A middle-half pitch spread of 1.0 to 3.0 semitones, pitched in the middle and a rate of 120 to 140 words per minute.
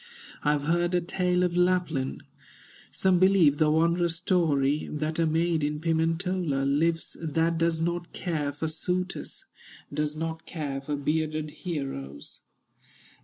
Yes: narrow, 2.5 semitones; medium, 160 Hz; slow, 135 wpm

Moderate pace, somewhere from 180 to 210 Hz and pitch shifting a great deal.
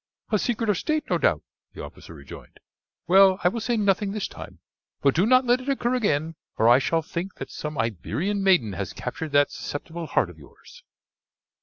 Yes: average, 195 wpm; high, 190 Hz; wide, 7.3 semitones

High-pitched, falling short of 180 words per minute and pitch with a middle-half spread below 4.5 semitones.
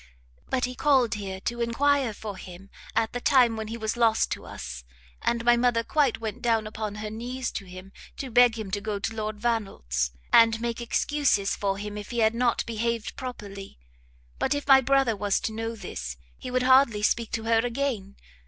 No: high, 225 Hz; average, 200 wpm; average, 2.8 semitones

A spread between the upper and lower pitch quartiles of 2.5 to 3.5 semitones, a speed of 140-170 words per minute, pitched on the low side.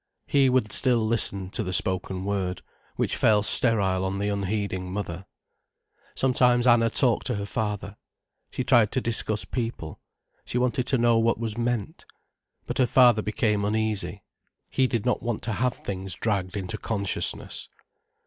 Yes: average, 3.2 semitones; average, 160 wpm; low, 110 Hz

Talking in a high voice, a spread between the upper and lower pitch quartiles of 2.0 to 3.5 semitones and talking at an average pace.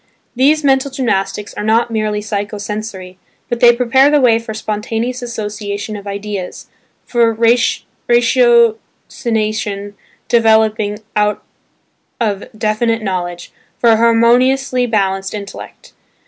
No: high, 220 Hz; narrow, 2.5 semitones; slow, 110 wpm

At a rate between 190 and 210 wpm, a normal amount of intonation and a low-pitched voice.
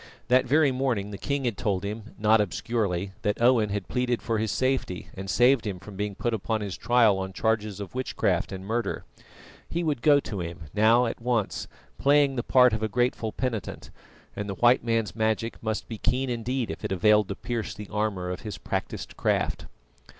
Yes: average, 200 wpm; average, 3.3 semitones; low, 110 Hz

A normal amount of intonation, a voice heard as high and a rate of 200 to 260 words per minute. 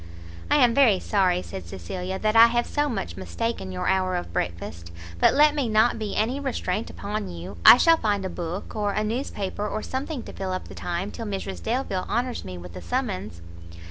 Yes: average, 4.7 semitones; high, 205 Hz; fast, 205 wpm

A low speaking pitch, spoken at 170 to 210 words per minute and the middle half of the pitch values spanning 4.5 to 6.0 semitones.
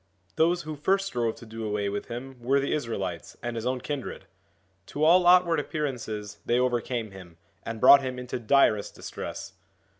Yes: low, 125 Hz; average, 175 wpm; average, 4.8 semitones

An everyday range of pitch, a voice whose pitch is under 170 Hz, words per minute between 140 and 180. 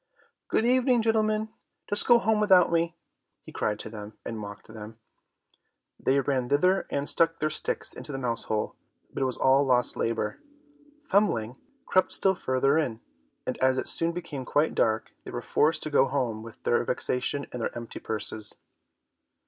No: wide, 6.7 semitones; low, 135 Hz; average, 175 wpm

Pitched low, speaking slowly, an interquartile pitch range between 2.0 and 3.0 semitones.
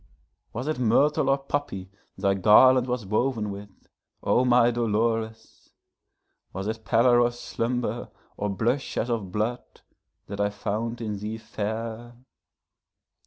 Yes: low, 115 Hz; slow, 125 wpm; narrow, 2.6 semitones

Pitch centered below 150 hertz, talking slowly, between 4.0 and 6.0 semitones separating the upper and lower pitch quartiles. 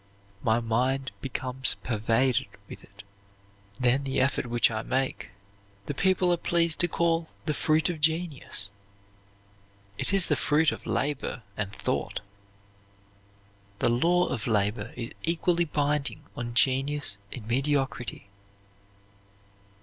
Yes: low, 135 Hz; slow, 125 wpm; average, 5.1 semitones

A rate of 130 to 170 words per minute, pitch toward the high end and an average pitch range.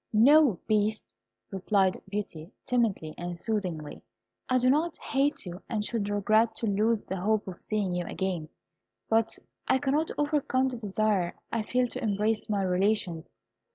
Yes: average, 155 wpm; high, 210 Hz; average, 3.6 semitones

